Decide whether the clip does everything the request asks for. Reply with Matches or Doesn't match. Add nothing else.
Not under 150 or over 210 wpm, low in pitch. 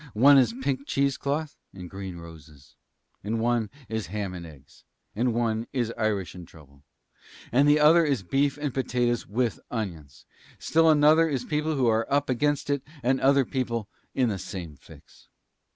Matches